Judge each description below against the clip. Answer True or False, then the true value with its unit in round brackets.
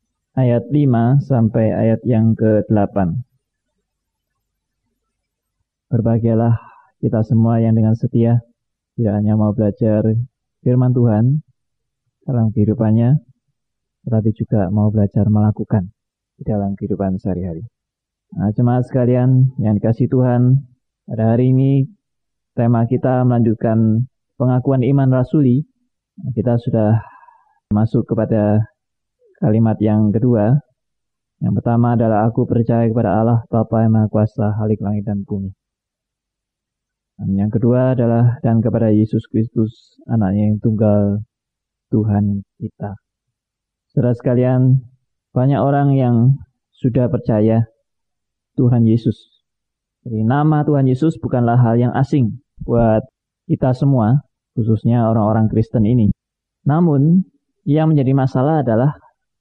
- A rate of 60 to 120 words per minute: True (110 wpm)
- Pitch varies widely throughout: False (2.8 semitones)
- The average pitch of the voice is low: True (115 Hz)